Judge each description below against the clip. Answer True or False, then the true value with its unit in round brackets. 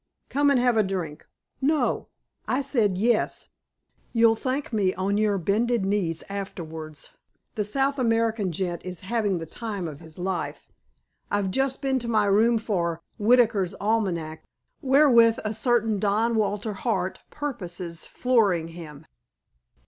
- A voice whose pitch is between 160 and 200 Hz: False (210 Hz)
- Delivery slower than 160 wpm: True (140 wpm)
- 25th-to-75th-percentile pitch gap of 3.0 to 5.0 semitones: True (4.4 semitones)